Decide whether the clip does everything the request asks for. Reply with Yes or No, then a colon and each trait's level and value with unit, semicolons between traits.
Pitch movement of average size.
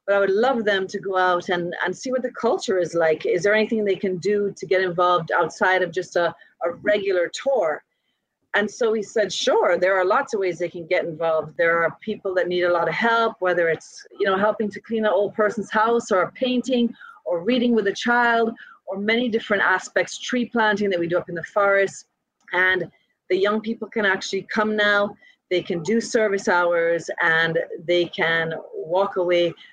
Yes: average, 3.7 semitones